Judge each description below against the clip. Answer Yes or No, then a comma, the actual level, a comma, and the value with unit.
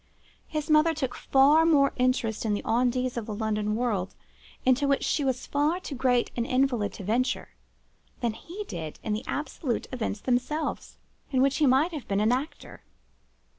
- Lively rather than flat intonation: No, average, 4.2 semitones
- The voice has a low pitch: No, very high, 255 Hz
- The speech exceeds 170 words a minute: Yes, average, 180 wpm